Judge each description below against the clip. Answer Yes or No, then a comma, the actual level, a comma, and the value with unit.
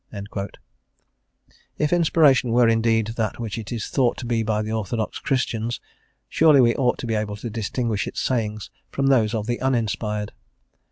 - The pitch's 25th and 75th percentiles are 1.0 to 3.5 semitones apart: Yes, narrow, 2.5 semitones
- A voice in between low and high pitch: No, low, 115 Hz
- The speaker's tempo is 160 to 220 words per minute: Yes, average, 180 wpm